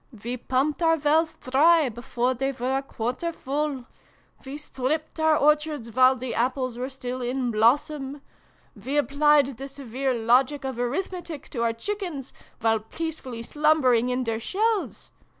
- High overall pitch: Yes, very high, 270 Hz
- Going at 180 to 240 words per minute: No, average, 150 wpm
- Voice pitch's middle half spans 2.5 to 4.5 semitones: Yes, average, 3.6 semitones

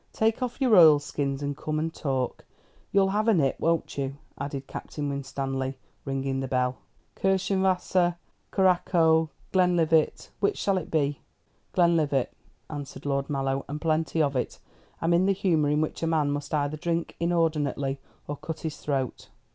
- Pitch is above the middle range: No, medium, 155 Hz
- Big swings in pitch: No, average, 3.8 semitones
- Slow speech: No, average, 155 wpm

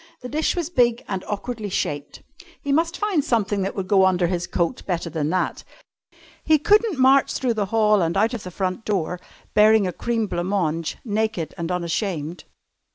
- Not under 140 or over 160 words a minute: No, average, 185 wpm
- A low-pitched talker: No, high, 205 Hz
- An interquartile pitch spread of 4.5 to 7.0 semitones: Yes, average, 5.0 semitones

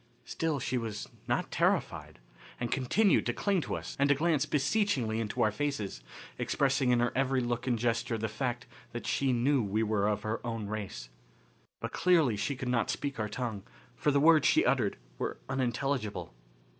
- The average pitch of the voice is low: Yes, low, 125 Hz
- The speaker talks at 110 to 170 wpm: No, average, 180 wpm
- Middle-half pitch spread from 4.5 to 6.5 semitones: No, average, 4.1 semitones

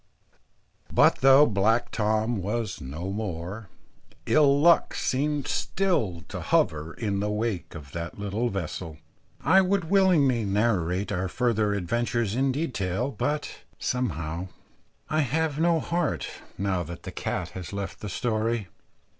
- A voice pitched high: No, low, 110 Hz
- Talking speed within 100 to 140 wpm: Yes, slow, 135 wpm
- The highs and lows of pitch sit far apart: Yes, wide, 6.4 semitones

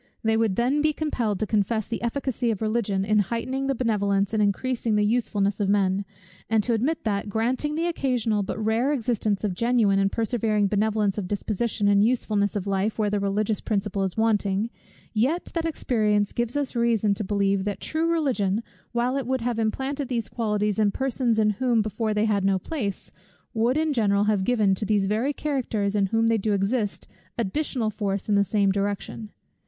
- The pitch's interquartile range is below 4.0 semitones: Yes, average, 3.0 semitones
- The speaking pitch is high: Yes, high, 215 Hz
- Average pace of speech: Yes, average, 190 wpm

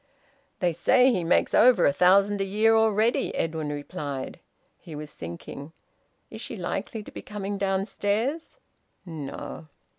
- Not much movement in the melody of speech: No, average, 5.3 semitones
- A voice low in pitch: No, high, 195 Hz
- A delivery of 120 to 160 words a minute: Yes, average, 140 wpm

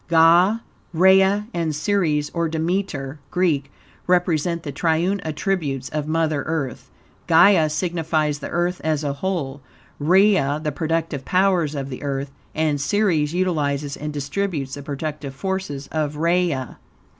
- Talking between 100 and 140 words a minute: Yes, slow, 135 wpm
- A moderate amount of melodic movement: Yes, average, 3.7 semitones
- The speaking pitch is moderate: Yes, medium, 160 Hz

